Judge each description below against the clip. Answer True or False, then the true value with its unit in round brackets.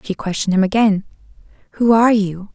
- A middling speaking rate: True (165 wpm)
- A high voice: True (205 Hz)